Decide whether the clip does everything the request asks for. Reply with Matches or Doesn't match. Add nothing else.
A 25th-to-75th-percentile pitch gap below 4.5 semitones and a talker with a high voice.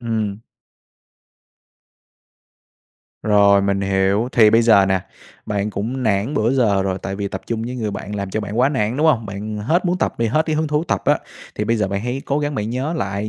Doesn't match